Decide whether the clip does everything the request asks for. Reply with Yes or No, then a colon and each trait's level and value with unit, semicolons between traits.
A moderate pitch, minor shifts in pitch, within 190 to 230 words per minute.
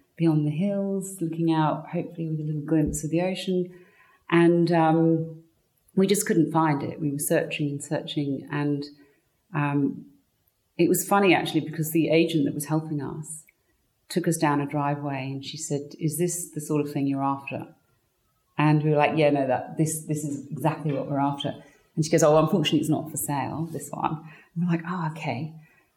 Yes: medium, 155 Hz; narrow, 2.2 semitones; average, 195 wpm